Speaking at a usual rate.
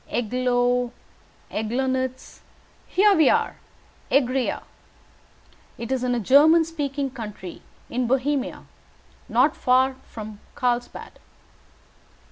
No: slow, 95 wpm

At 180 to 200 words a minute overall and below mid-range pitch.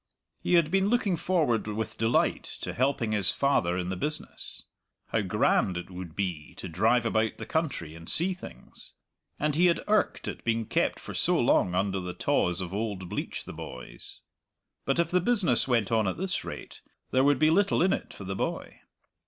Yes: average, 195 wpm; low, 115 Hz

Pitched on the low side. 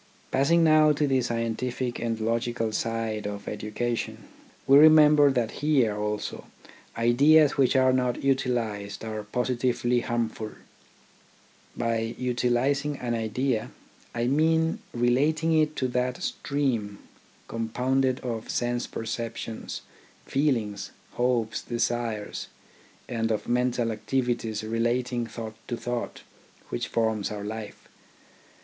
Yes: low, 120 Hz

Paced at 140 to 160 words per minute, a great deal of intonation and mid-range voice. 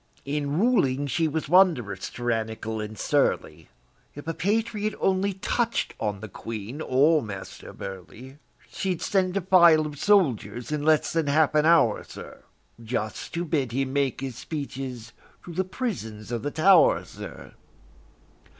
Yes: average, 150 wpm; wide, 6.9 semitones; medium, 145 Hz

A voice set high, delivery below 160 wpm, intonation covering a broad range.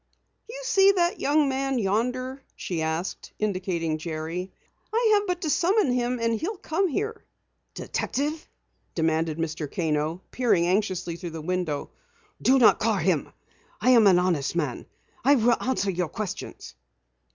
Yes: high, 215 Hz; average, 150 wpm; wide, 8.7 semitones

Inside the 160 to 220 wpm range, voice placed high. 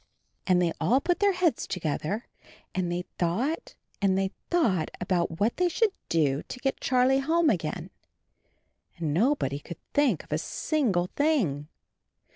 Yes: average, 165 wpm; high, 195 Hz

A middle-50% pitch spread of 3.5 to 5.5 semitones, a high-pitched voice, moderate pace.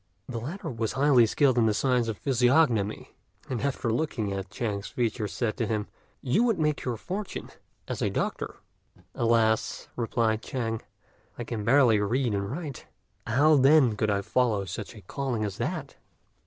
No: average, 3.8 semitones; low, 120 Hz; average, 170 wpm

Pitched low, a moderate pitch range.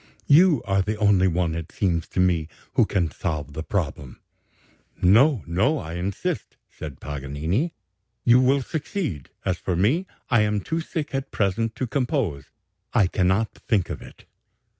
No: low, 100 Hz; wide, 7.2 semitones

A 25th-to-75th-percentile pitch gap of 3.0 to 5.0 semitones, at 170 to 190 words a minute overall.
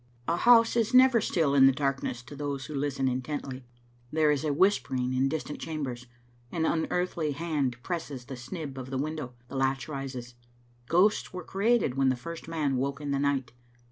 Yes: average, 3.7 semitones; average, 180 wpm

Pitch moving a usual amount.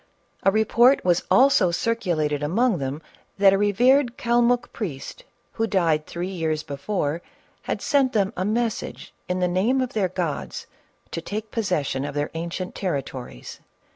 No: wide, 6.3 semitones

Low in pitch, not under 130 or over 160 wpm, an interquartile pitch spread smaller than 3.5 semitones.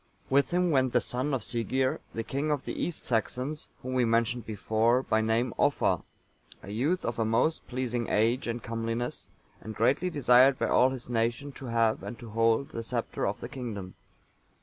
No: low, 120 Hz; average, 190 wpm; narrow, 2.6 semitones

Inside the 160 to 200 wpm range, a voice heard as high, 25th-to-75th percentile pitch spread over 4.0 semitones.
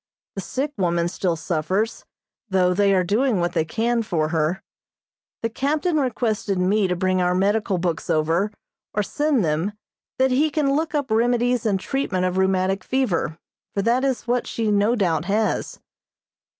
Yes: average, 165 wpm; high, 200 Hz; average, 5.2 semitones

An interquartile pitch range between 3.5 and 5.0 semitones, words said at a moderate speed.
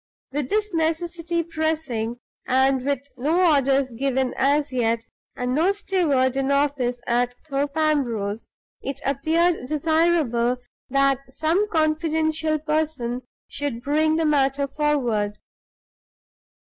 No: average, 3.8 semitones; slow, 110 wpm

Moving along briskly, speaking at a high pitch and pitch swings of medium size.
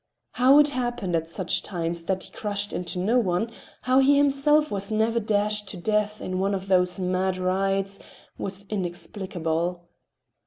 No: average, 155 wpm; high, 195 Hz; average, 3.2 semitones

